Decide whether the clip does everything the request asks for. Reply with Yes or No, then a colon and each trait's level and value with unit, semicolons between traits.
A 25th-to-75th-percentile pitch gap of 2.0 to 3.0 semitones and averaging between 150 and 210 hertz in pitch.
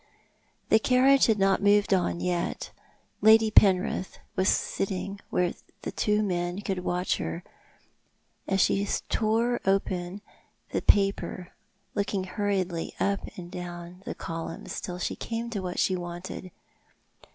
Yes: narrow, 2.6 semitones; high, 190 Hz